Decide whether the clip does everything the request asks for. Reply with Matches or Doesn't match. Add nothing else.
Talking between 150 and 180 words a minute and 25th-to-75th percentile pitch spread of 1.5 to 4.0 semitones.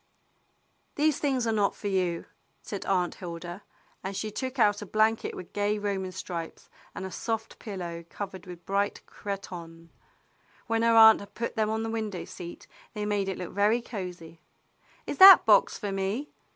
Matches